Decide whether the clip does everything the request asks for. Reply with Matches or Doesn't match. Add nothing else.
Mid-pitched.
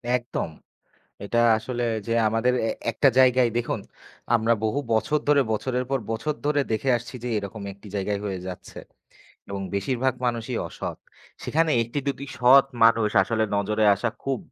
Doesn't match